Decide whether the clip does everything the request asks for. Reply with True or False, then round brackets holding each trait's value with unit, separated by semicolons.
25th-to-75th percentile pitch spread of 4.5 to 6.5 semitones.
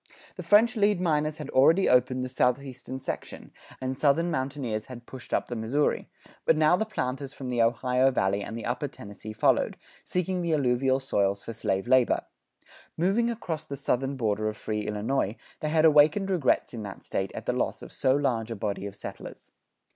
True (5.0 semitones)